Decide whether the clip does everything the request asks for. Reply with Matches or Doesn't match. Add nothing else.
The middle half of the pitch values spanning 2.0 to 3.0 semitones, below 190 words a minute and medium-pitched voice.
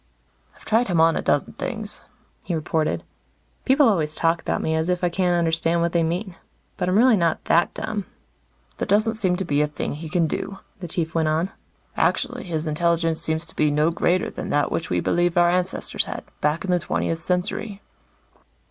Doesn't match